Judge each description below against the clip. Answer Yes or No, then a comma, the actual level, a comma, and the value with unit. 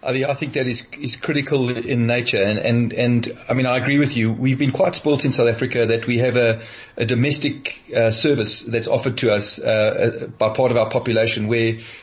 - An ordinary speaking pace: No, fast, 225 wpm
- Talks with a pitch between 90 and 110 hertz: No, low, 120 Hz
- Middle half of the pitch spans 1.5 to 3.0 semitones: Yes, average, 2.7 semitones